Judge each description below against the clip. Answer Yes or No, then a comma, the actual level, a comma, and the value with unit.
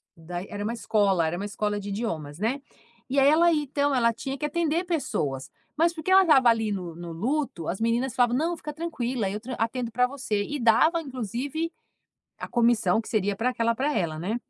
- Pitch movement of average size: No, wide, 5.9 semitones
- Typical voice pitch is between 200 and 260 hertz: Yes, high, 235 Hz